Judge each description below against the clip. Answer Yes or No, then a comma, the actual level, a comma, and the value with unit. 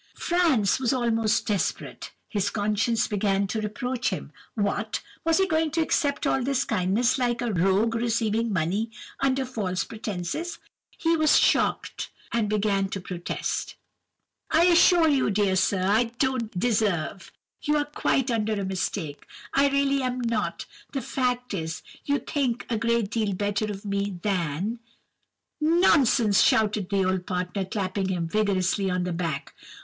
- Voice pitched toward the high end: Yes, high, 215 Hz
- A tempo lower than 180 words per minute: Yes, average, 145 wpm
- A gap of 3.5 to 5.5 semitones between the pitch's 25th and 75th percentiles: Yes, average, 4.6 semitones